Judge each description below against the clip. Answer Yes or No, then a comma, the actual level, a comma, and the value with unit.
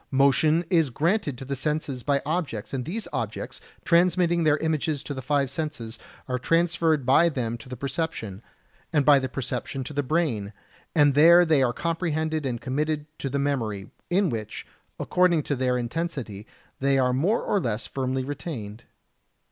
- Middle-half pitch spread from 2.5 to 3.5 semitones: No, average, 4.2 semitones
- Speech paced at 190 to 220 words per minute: No, average, 170 wpm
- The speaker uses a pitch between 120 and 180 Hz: Yes, medium, 140 Hz